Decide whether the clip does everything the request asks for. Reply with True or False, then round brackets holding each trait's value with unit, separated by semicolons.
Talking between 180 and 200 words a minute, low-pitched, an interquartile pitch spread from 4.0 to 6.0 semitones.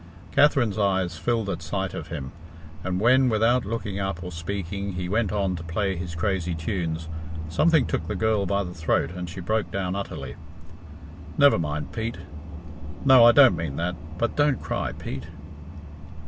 False (170 wpm; 95 Hz; 4.4 semitones)